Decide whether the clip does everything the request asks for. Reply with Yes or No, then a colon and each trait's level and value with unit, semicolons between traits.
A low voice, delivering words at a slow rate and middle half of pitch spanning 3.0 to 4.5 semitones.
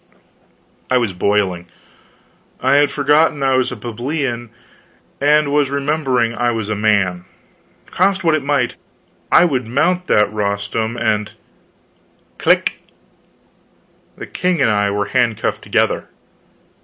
No: low, 120 Hz; slow, 125 wpm; wide, 5.5 semitones